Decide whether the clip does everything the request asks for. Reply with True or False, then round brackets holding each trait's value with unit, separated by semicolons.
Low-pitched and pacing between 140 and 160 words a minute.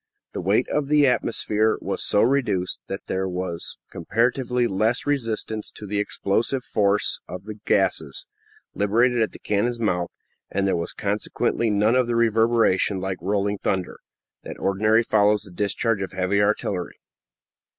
True (105 Hz; 150 wpm)